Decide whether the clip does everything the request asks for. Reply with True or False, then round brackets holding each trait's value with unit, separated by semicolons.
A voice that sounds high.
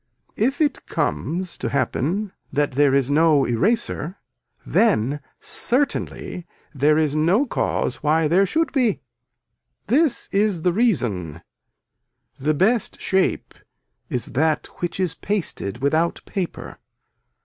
False (170 Hz)